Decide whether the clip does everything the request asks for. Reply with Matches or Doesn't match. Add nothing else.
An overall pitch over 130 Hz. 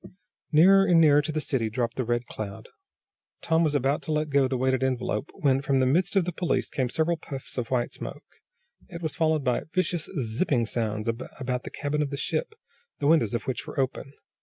Matches